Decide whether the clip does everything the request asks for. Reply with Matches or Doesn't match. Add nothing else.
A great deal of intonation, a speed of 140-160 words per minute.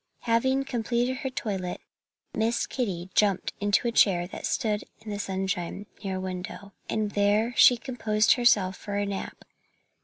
Doesn't match